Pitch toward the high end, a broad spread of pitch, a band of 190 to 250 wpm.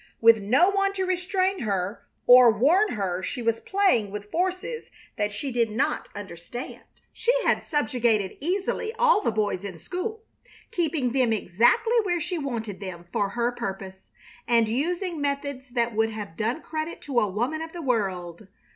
No: high, 245 Hz; wide, 8.9 semitones; average, 165 wpm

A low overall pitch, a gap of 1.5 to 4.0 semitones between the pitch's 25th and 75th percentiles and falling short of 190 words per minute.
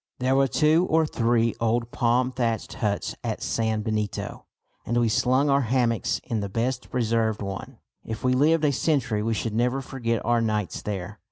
Yes: low, 115 Hz; average, 2.7 semitones; average, 180 wpm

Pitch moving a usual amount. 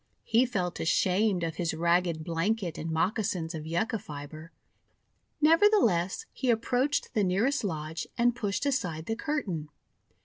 No: wide, 6.2 semitones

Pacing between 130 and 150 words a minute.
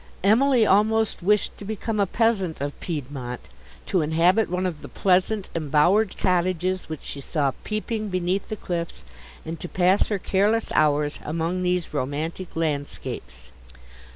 Yes: average, 145 wpm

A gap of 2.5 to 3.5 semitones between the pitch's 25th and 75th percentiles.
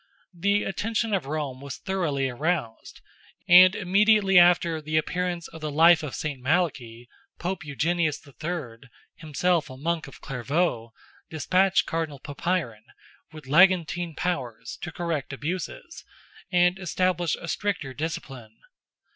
No: average, 4.3 semitones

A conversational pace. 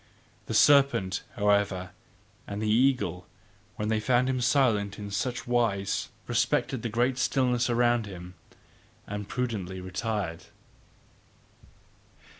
No: slow, 110 wpm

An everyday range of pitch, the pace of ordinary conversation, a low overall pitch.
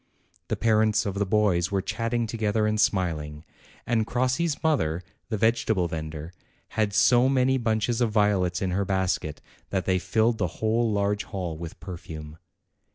Yes: average, 4.0 semitones; average, 160 wpm; low, 105 Hz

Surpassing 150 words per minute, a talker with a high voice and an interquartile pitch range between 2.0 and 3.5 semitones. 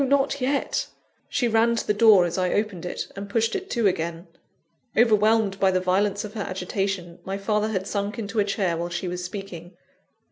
Yes: average, 200 wpm; high, 200 Hz; average, 3.1 semitones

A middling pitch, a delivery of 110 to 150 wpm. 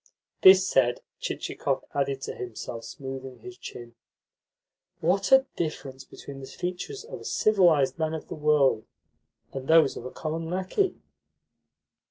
Yes: medium, 150 Hz; average, 140 wpm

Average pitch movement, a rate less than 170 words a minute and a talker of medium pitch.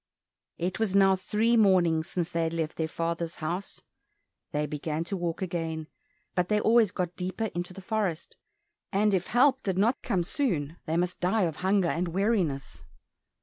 No: average, 3.3 semitones; average, 175 wpm; medium, 180 Hz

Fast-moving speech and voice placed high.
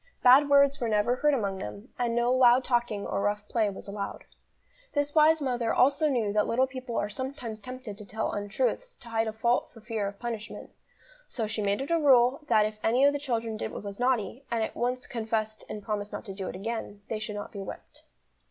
Yes: fast, 225 wpm; high, 230 Hz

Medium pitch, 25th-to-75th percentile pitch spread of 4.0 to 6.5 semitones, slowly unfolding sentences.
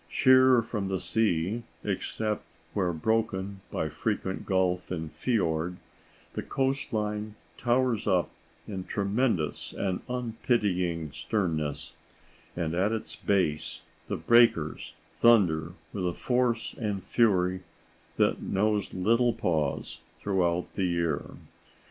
No: low, 100 Hz; average, 4.3 semitones; slow, 110 wpm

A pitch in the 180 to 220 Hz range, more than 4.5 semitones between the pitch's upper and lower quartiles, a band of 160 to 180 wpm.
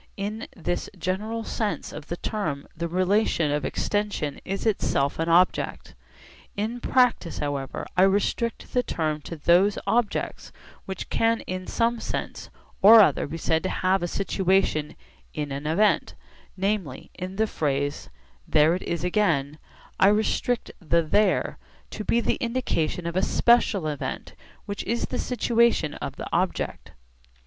No: medium, 185 Hz; average, 5.3 semitones; average, 150 wpm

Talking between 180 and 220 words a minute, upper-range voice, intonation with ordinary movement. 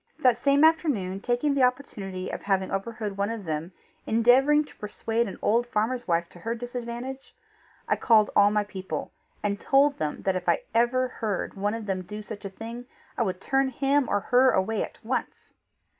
Yes: average, 190 wpm; high, 225 Hz; average, 4.4 semitones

